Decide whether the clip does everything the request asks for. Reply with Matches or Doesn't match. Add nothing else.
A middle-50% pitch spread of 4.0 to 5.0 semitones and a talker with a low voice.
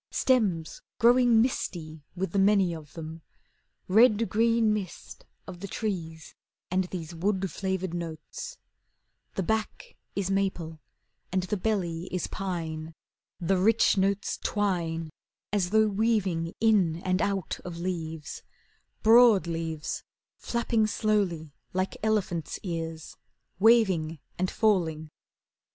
Doesn't match